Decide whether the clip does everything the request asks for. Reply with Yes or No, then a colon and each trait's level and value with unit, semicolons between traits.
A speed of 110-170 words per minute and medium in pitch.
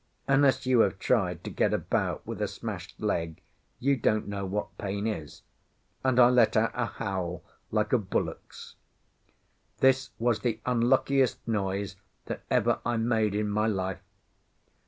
No: average, 155 wpm; low, 110 Hz